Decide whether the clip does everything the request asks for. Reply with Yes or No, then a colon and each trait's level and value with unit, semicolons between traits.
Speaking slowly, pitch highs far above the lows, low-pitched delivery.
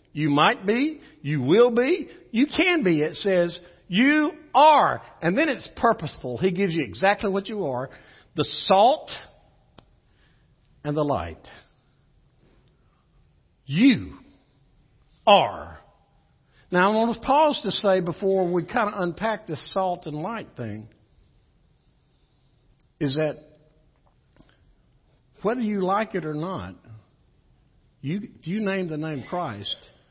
No: slow, 125 wpm; wide, 6.4 semitones; medium, 185 Hz